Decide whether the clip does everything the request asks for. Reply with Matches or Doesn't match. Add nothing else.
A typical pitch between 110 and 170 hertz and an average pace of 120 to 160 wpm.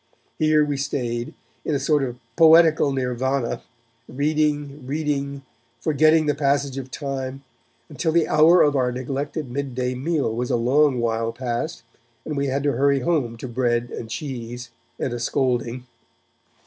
Matches